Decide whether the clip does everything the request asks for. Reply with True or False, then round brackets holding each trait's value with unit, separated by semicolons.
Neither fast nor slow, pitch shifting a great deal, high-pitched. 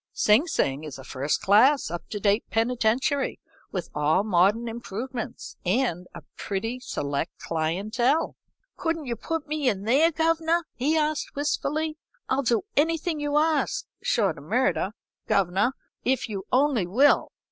True (145 wpm; 7.2 semitones; 245 Hz)